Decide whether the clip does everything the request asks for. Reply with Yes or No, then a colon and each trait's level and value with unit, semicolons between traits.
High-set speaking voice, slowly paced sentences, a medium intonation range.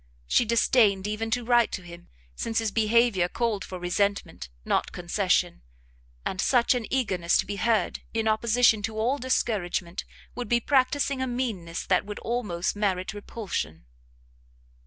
No: high, 220 Hz; average, 150 wpm; average, 4.1 semitones